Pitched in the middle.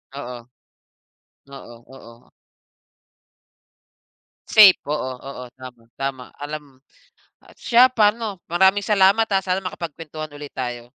Yes: medium, 150 Hz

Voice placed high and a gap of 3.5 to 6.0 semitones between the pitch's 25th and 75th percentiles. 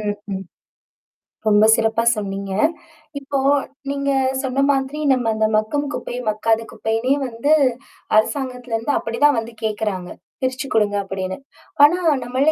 Yes: high, 230 Hz; average, 4.0 semitones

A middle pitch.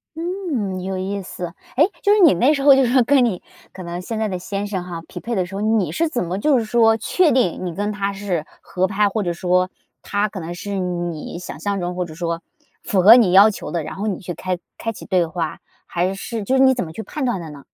No: high, 195 Hz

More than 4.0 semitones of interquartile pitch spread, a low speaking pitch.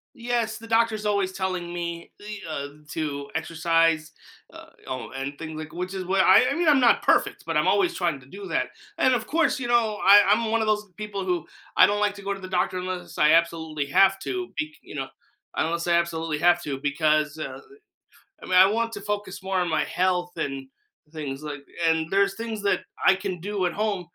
No: average, 4.5 semitones; medium, 185 Hz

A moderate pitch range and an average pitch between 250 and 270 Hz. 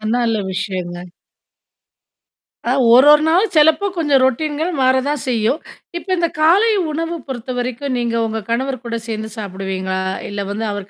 No: wide, 5.8 semitones; very high, 255 Hz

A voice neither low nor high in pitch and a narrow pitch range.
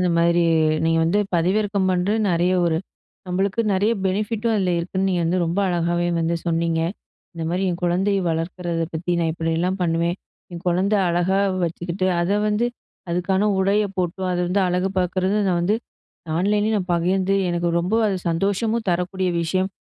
Yes: medium, 180 Hz; narrow, 2.2 semitones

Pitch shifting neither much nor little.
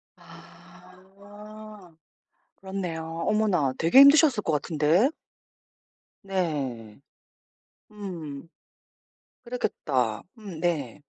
Yes: average, 4.8 semitones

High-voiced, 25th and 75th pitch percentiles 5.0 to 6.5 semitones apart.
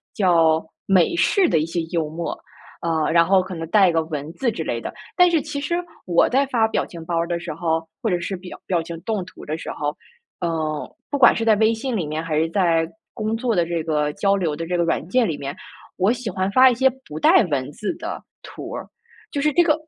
No: medium, 175 Hz; wide, 5.5 semitones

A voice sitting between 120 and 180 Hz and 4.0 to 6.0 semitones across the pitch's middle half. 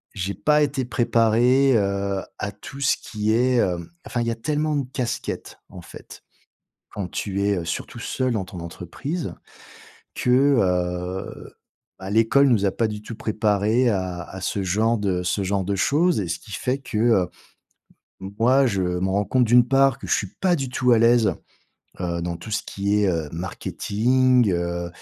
No: low, 105 Hz; average, 4.9 semitones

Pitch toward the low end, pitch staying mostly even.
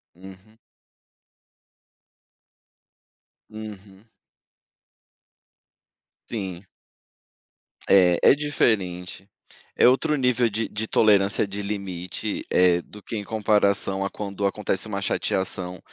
Yes: low, 100 Hz; narrow, 2.2 semitones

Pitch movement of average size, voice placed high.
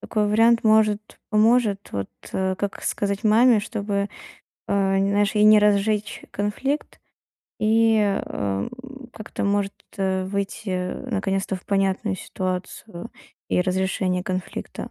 No: narrow, 2.1 semitones; high, 200 Hz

